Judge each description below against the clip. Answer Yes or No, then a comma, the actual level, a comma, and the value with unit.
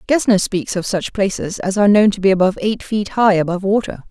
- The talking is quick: Yes, fast, 235 wpm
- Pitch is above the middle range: Yes, high, 200 Hz